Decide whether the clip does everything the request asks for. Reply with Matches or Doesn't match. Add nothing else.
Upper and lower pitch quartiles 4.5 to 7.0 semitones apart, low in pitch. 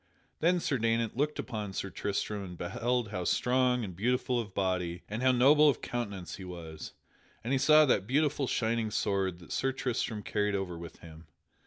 Matches